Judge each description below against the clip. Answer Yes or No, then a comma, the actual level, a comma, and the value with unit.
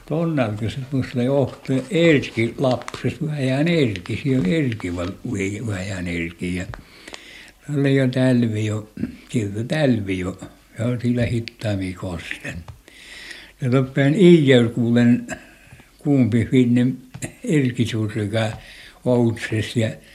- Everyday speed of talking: Yes, average, 105 wpm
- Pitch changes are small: No, average, 3.7 semitones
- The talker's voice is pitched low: Yes, low, 120 Hz